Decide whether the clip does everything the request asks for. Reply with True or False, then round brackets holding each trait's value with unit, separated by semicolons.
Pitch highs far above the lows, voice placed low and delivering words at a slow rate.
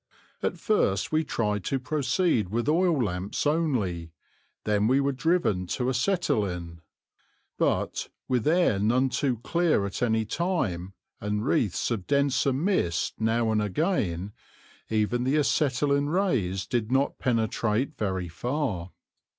True (6.2 semitones; 120 Hz; 130 wpm)